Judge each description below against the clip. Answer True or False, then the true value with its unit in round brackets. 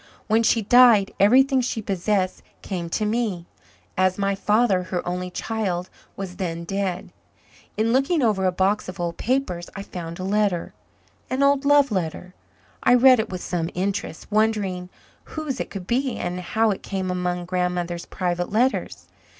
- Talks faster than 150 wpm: True (165 wpm)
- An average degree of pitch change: True (4.0 semitones)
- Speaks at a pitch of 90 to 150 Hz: False (195 Hz)